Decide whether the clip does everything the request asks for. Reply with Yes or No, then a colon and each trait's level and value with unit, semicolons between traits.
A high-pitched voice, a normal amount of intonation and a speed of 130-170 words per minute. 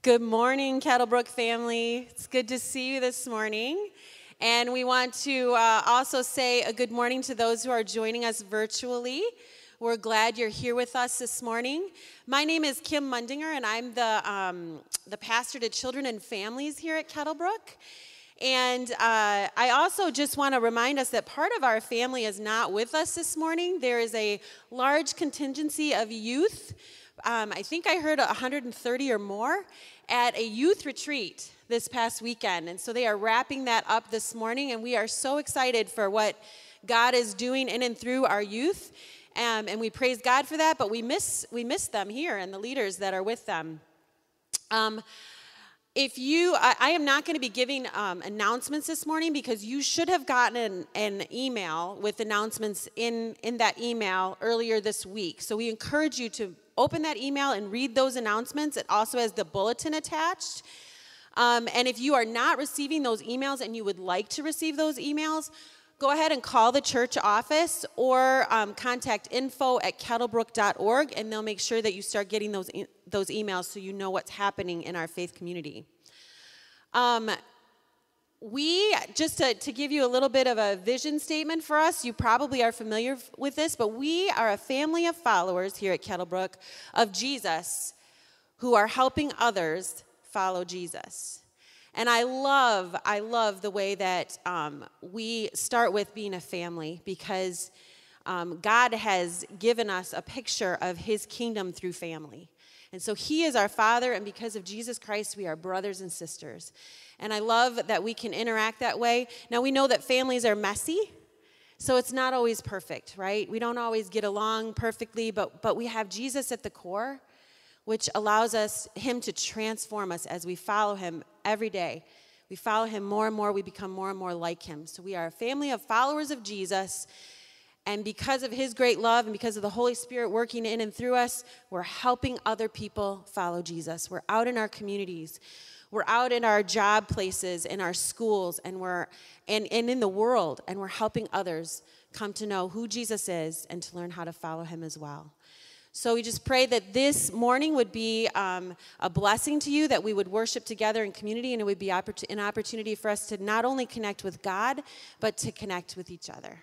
No: high, 230 Hz; average, 4.0 semitones; average, 190 wpm